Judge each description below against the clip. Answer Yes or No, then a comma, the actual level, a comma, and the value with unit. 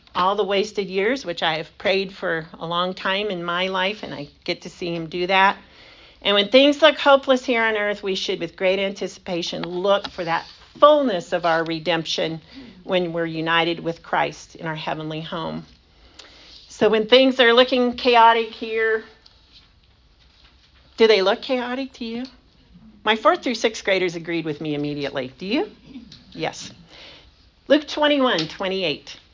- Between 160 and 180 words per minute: Yes, average, 170 wpm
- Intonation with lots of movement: Yes, wide, 5.7 semitones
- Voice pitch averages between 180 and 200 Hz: Yes, high, 190 Hz